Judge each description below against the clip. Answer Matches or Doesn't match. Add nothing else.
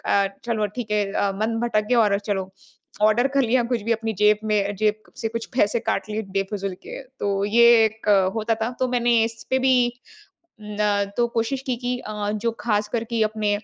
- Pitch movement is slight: Matches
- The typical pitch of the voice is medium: Doesn't match